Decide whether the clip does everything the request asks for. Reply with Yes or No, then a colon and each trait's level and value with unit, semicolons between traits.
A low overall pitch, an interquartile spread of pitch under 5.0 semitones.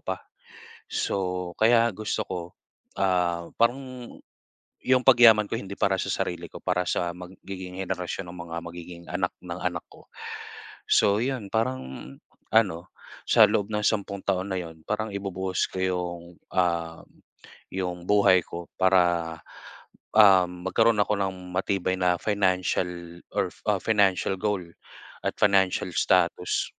Yes: very low, 95 Hz; average, 2.7 semitones